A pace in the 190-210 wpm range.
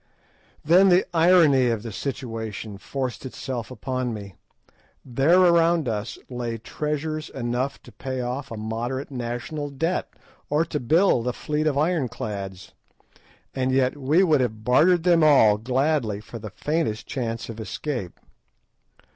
No: average, 140 wpm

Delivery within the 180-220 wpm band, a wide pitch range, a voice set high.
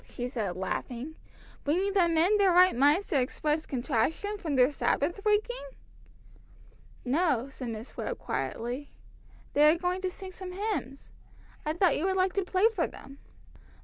No: average, 160 wpm; wide, 6.0 semitones; very high, 325 Hz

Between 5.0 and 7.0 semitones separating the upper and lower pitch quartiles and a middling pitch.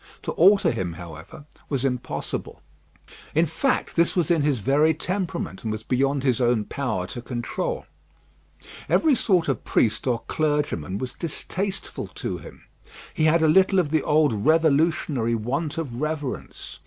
Yes: wide, 5.5 semitones; medium, 145 Hz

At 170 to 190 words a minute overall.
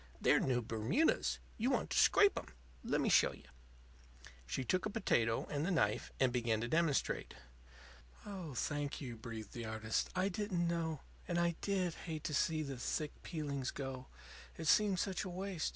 Yes: average, 175 wpm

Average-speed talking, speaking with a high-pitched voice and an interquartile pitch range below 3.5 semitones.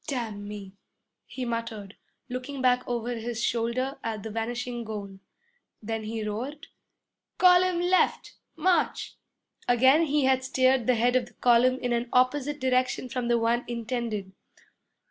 Yes: average, 145 wpm; high, 245 Hz; narrow, 2.4 semitones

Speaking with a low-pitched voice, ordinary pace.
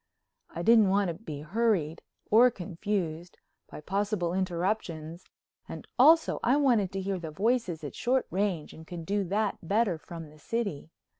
No: high, 190 Hz; average, 160 wpm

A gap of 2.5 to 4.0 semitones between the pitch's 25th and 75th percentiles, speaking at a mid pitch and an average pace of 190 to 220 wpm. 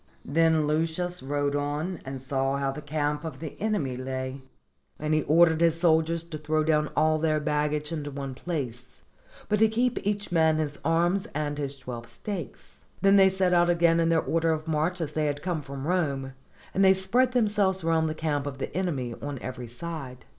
Yes: average, 3.2 semitones; medium, 155 Hz; average, 195 wpm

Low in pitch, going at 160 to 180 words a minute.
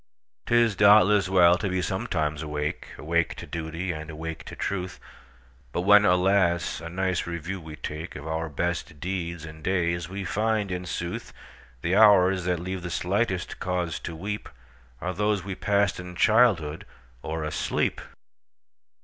No: very low, 90 Hz; average, 140 wpm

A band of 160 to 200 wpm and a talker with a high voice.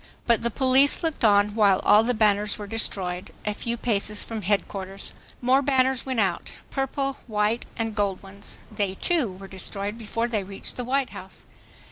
Yes: average, 170 wpm; high, 215 Hz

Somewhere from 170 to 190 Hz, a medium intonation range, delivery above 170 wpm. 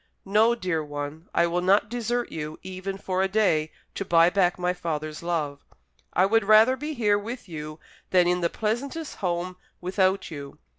Yes: medium, 185 Hz; average, 4.2 semitones; average, 180 wpm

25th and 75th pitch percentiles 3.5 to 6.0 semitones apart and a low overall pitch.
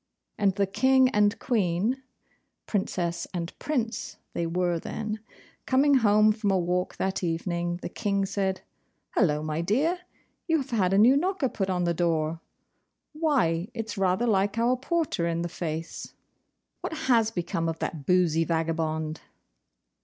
No: wide, 5.4 semitones; high, 190 Hz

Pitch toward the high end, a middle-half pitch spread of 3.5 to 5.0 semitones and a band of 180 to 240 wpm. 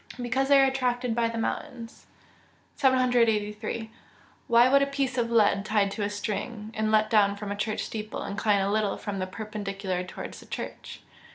No: high, 220 Hz; average, 3.0 semitones; average, 185 wpm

